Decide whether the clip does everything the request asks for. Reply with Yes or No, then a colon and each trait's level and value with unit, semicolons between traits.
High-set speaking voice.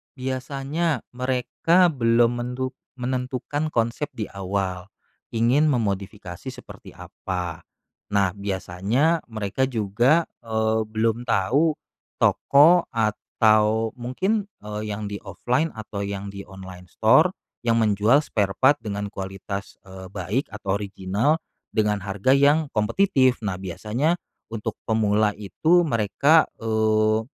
No: low, 110 Hz